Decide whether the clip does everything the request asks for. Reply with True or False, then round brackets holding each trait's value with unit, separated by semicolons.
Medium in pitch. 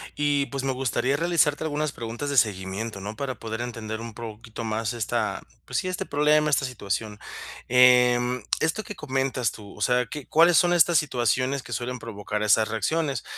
False (125 Hz)